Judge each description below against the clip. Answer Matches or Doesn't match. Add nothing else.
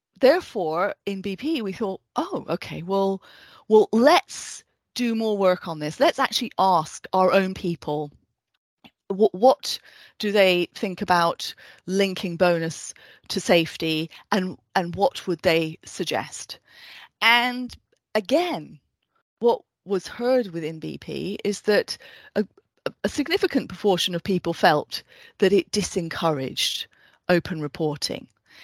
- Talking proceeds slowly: Matches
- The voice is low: Doesn't match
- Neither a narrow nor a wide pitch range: Matches